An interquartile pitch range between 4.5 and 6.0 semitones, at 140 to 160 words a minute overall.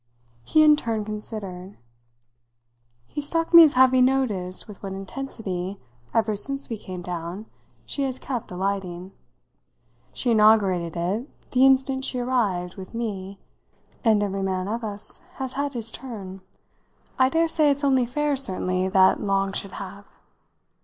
Yes: wide, 5.5 semitones; average, 145 wpm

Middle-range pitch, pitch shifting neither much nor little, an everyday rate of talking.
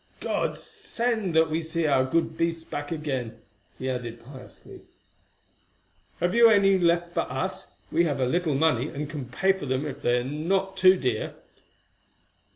No: medium, 160 Hz; wide, 5.8 semitones; average, 165 wpm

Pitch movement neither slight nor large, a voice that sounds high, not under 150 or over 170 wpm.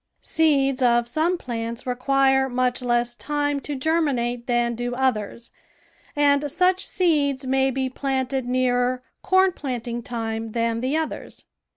No: average, 3.0 semitones; very high, 260 Hz; slow, 135 wpm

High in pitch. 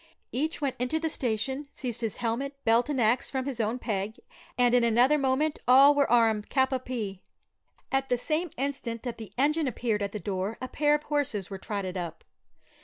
Yes: very high, 250 Hz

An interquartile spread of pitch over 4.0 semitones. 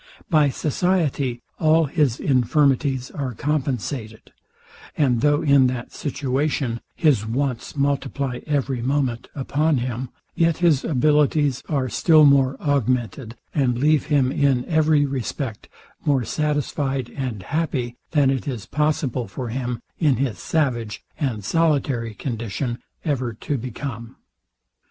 No: average, 3.2 semitones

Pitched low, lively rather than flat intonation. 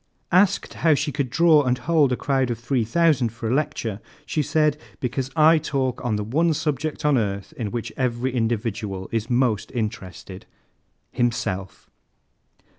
No: low, 125 Hz; average, 4.8 semitones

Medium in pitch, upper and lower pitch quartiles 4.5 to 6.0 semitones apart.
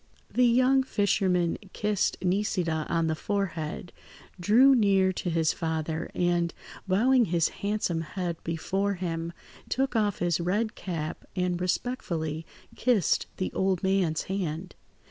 No: medium, 180 Hz; average, 3.6 semitones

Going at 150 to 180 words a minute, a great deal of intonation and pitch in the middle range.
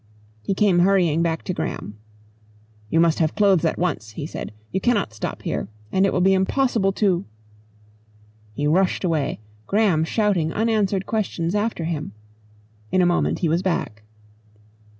No: average, 160 wpm; average, 4.0 semitones; medium, 175 Hz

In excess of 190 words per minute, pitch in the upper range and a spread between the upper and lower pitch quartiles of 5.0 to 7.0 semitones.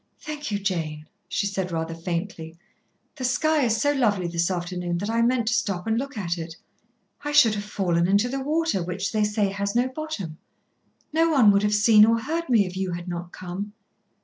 Yes: fast, 205 wpm; high, 205 Hz; wide, 5.6 semitones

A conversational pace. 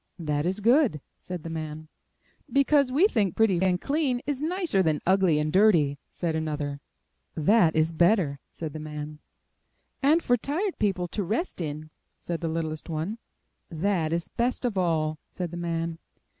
Yes: average, 180 wpm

